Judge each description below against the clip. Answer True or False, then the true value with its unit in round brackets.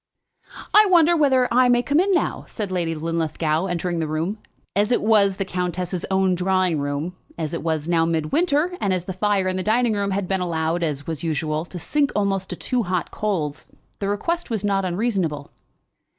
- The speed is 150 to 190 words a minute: False (200 wpm)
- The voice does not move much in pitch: False (4.5 semitones)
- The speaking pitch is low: False (185 Hz)